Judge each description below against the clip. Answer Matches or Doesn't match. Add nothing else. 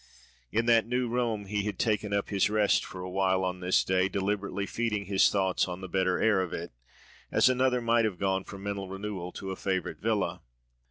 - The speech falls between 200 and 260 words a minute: Matches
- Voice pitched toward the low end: Matches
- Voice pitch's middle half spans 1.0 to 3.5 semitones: Matches